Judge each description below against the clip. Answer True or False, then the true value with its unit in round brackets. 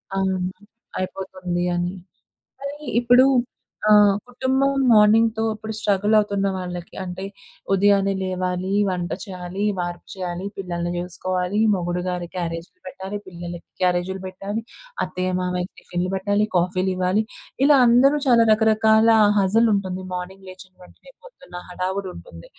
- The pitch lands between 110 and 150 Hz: False (190 Hz)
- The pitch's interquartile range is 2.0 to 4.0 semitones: True (2.8 semitones)